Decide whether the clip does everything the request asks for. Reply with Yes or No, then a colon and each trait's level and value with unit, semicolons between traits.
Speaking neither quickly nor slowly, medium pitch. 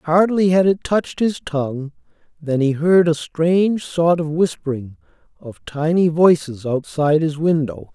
Yes: average, 150 wpm; medium, 160 Hz